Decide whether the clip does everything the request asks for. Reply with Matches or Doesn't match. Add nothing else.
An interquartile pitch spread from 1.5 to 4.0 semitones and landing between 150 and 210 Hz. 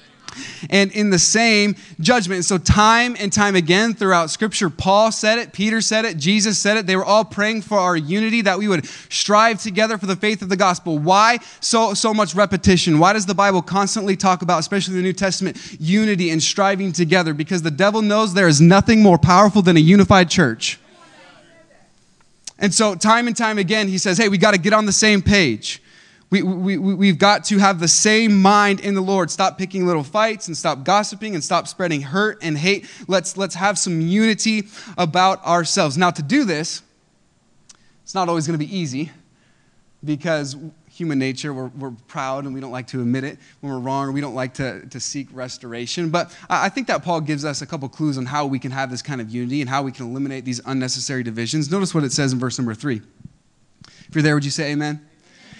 Doesn't match